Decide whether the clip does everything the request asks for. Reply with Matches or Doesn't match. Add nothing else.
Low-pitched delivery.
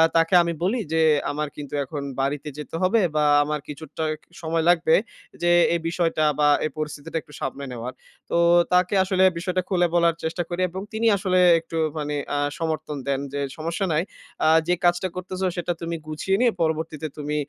Doesn't match